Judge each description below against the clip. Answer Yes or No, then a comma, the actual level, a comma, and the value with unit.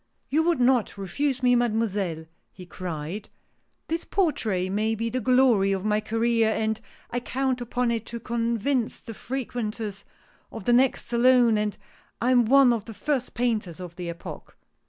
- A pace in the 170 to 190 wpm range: Yes, average, 175 wpm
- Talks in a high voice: Yes, high, 230 Hz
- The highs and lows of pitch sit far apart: No, average, 3.2 semitones